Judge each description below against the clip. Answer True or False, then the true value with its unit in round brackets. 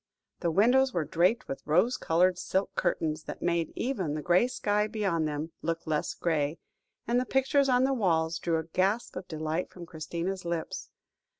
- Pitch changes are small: False (4.9 semitones)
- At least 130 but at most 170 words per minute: False (180 wpm)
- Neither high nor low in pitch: True (175 Hz)